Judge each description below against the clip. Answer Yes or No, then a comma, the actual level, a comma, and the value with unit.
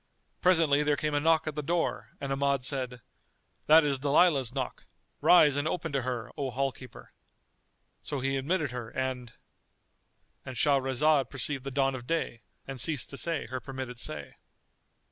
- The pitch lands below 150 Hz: Yes, low, 135 Hz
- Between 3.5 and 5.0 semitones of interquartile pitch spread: No, narrow, 2.6 semitones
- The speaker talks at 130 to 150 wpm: No, average, 165 wpm